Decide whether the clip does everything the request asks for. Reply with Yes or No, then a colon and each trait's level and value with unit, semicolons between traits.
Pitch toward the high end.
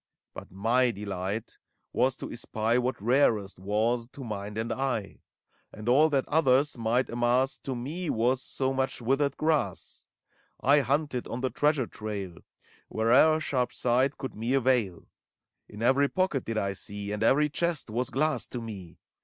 No: low, 125 Hz